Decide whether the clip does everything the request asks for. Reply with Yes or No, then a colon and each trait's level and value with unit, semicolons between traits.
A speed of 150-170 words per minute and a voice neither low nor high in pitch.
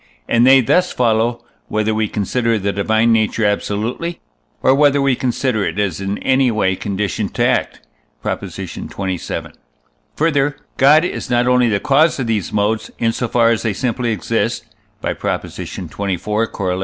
No: average, 165 wpm; low, 115 Hz